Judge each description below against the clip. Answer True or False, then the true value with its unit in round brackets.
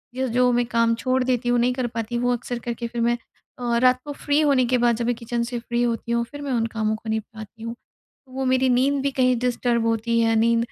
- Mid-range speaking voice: False (240 Hz)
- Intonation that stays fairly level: True (1.5 semitones)